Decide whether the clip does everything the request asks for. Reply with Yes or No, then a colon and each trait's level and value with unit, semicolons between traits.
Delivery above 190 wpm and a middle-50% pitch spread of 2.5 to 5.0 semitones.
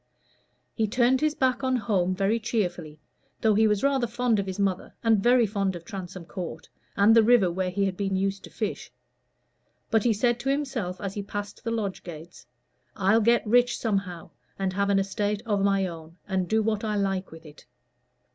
Yes: average, 200 wpm; average, 3.3 semitones